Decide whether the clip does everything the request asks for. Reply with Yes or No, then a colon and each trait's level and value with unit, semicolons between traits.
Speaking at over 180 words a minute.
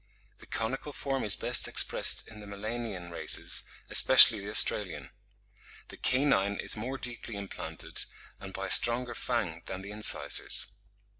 No: average, 145 wpm